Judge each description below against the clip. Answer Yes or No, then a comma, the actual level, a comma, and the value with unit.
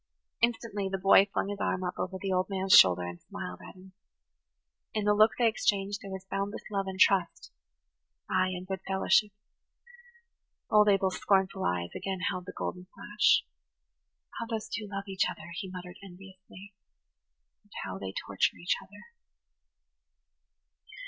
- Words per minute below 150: No, average, 155 wpm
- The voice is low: No, high, 190 Hz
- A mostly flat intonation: Yes, narrow, 1.8 semitones